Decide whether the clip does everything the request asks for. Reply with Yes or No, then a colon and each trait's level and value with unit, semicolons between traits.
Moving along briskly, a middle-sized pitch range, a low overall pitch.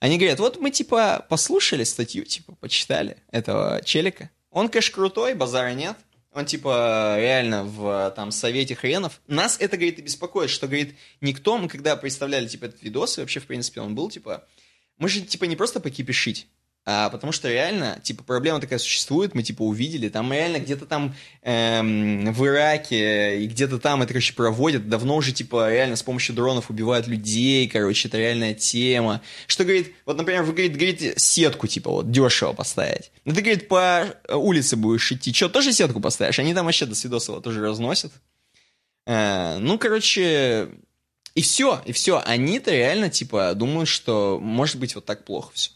No: fast, 175 wpm; wide, 6.0 semitones; low, 130 Hz